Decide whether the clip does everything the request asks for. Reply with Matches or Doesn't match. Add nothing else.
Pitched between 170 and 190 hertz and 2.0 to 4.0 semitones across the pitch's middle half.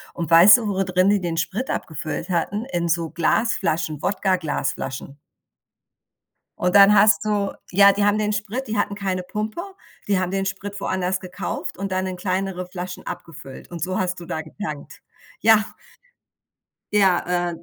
Matches